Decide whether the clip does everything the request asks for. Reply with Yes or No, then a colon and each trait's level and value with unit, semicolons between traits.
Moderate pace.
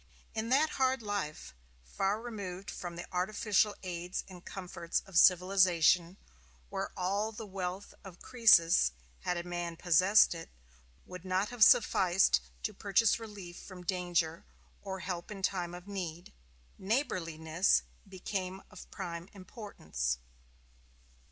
No: slow, 125 wpm